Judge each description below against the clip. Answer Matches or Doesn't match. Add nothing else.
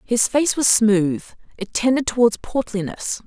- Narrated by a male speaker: Doesn't match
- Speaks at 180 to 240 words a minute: Doesn't match